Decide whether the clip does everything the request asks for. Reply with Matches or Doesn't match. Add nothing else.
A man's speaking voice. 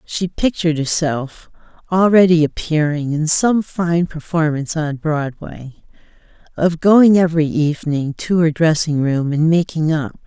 Doesn't match